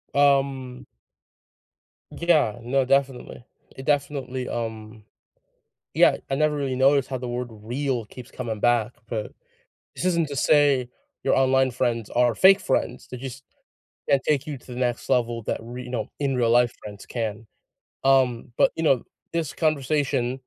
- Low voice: Yes, low, 130 Hz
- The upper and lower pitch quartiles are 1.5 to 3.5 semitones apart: Yes, narrow, 2.6 semitones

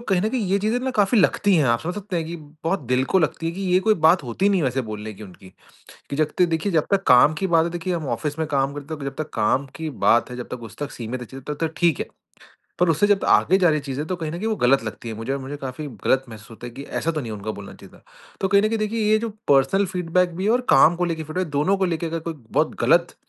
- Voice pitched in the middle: Yes, medium, 160 Hz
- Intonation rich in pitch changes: Yes, wide, 5.9 semitones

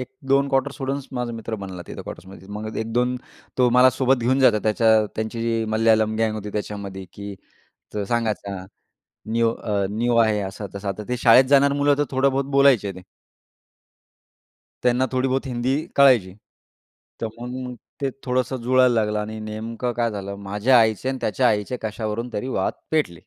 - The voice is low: Yes, low, 115 Hz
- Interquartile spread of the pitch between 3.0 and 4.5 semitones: Yes, average, 3.4 semitones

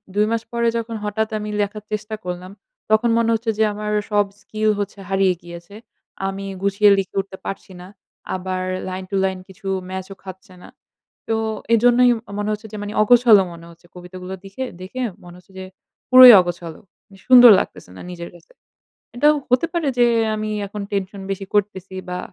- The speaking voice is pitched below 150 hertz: No, high, 205 Hz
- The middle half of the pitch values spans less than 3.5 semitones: Yes, average, 2.8 semitones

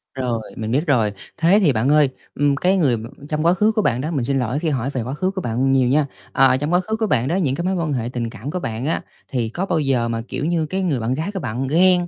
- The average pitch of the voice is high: No, medium, 140 Hz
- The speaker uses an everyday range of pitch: No, wide, 5.7 semitones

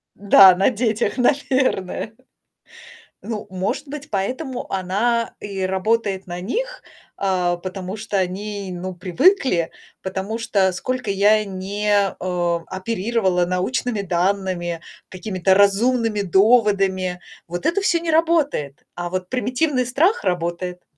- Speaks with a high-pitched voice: Yes, high, 200 Hz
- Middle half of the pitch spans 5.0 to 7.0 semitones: No, average, 4.3 semitones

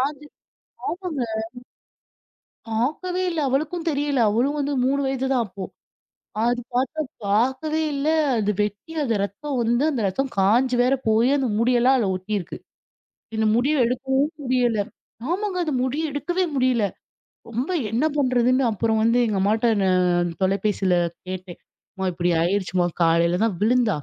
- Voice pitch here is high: Yes, high, 245 Hz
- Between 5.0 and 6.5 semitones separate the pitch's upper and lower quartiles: Yes, average, 5.3 semitones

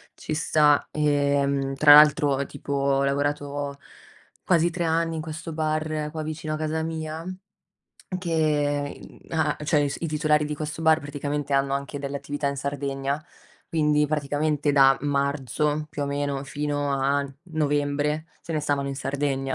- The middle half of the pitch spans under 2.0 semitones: Yes, narrow, 1.6 semitones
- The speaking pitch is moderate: Yes, medium, 145 Hz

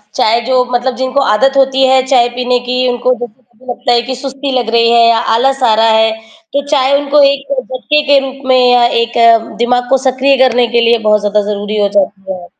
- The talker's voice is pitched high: Yes, very high, 250 Hz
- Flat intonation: Yes, narrow, 2.3 semitones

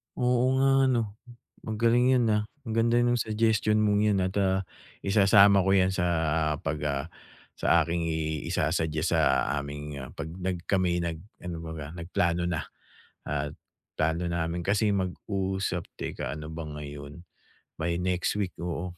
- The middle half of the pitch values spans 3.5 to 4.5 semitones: Yes, average, 4.2 semitones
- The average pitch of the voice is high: No, very low, 90 Hz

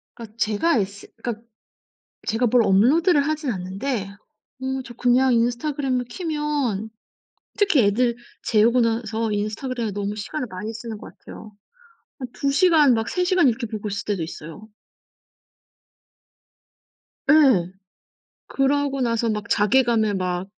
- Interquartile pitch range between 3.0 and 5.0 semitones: Yes, average, 4.4 semitones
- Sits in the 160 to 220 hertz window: No, high, 235 Hz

